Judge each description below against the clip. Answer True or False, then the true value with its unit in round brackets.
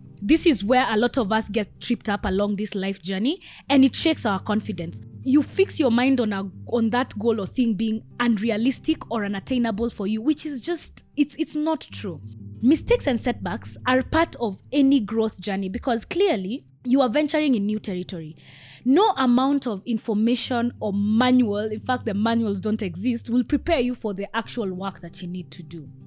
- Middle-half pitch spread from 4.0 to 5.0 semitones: True (4.5 semitones)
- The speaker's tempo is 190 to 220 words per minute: True (195 wpm)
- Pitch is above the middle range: True (230 Hz)